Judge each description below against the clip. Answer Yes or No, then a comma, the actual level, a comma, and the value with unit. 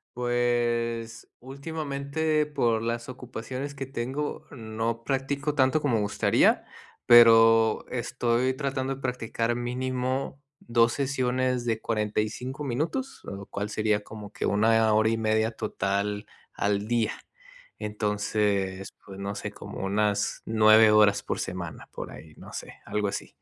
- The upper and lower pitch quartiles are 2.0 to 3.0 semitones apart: No, average, 3.4 semitones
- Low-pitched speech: Yes, low, 115 Hz